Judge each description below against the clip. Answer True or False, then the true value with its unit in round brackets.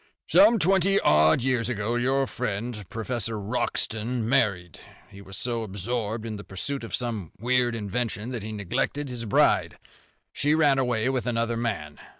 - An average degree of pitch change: True (3.3 semitones)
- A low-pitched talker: True (115 Hz)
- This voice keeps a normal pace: True (155 wpm)